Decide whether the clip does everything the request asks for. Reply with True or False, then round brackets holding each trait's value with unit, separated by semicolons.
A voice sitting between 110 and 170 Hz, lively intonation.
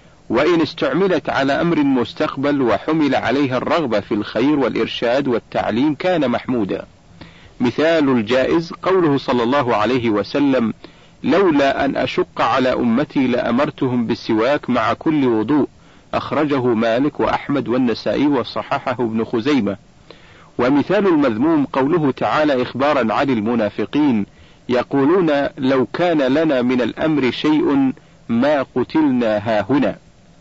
True (140 Hz; 6.8 semitones)